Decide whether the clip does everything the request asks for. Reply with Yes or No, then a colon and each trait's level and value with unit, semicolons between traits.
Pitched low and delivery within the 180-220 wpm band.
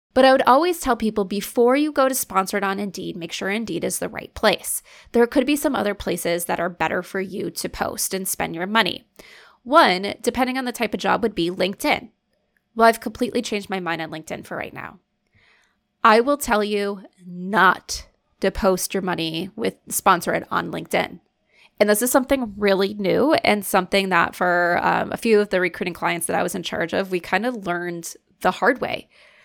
No: high, 205 Hz; fast, 205 wpm